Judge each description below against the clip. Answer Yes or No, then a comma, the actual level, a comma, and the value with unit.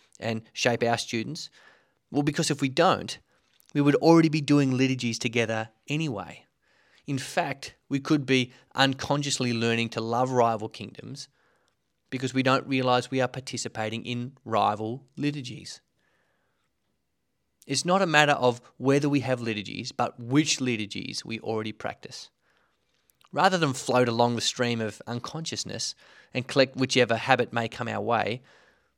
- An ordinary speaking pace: Yes, average, 145 wpm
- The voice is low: Yes, low, 125 Hz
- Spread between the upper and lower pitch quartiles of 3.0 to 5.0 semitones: Yes, average, 3.3 semitones